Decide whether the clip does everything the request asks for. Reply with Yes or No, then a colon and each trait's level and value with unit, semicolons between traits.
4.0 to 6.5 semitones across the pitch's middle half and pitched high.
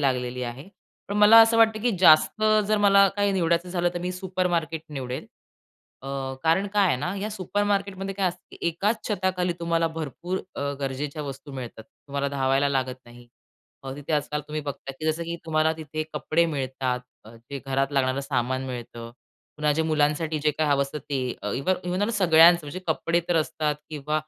No: average, 4.9 semitones; medium, 155 Hz